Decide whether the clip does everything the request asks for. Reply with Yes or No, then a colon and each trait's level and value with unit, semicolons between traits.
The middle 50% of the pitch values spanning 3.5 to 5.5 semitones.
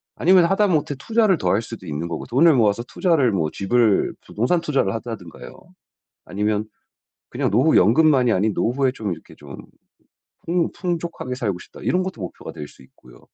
No: wide, 8.5 semitones